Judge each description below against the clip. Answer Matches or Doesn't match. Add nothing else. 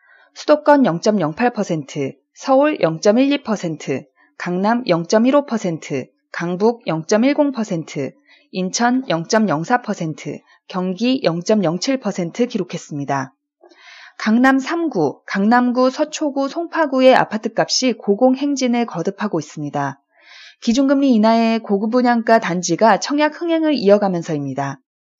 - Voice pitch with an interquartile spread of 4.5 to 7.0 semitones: Doesn't match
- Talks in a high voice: Matches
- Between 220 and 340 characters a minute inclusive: Doesn't match